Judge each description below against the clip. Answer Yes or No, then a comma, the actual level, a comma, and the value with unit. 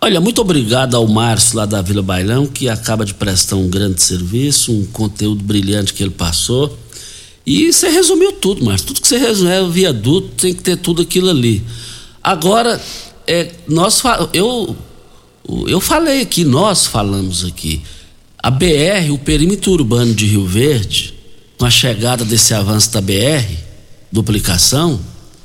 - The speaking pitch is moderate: No, low, 120 Hz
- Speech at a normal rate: Yes, average, 155 wpm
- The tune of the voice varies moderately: No, wide, 8.7 semitones